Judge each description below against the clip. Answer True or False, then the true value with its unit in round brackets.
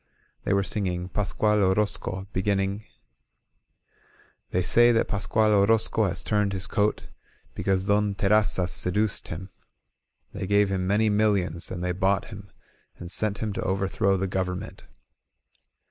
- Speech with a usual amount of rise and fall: False (2.0 semitones)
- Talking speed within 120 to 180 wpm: True (135 wpm)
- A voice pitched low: True (100 Hz)